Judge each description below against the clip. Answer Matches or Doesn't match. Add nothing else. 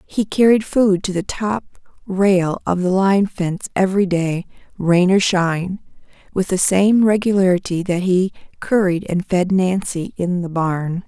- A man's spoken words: Doesn't match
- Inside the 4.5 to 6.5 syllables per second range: Doesn't match